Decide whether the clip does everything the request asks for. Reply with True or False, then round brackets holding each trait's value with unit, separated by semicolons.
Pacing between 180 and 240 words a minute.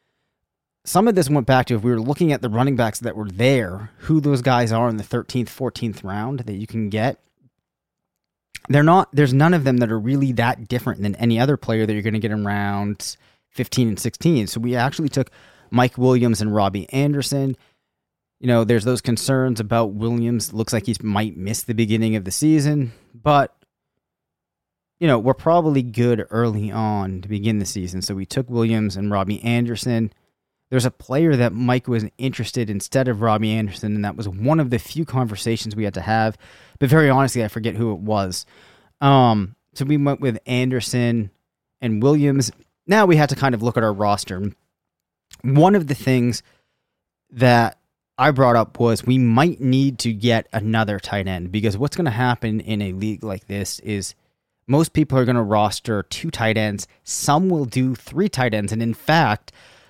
True (195 wpm)